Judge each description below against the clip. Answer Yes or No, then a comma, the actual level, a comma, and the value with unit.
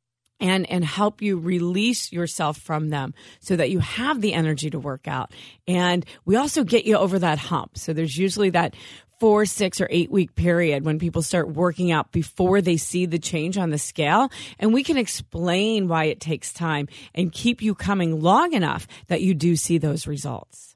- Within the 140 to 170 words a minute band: No, average, 195 wpm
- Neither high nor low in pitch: Yes, medium, 175 Hz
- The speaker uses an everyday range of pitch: Yes, average, 3.8 semitones